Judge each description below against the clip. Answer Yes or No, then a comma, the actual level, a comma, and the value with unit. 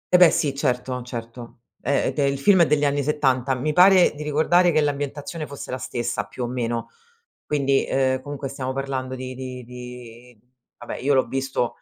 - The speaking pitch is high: No, low, 135 Hz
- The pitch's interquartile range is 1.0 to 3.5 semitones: Yes, average, 2.7 semitones